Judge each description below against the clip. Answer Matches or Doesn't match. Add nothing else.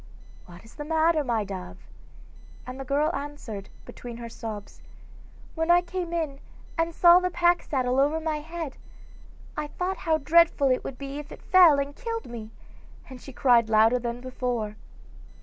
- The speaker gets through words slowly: Doesn't match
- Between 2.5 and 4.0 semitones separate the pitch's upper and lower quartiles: Doesn't match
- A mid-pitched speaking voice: Doesn't match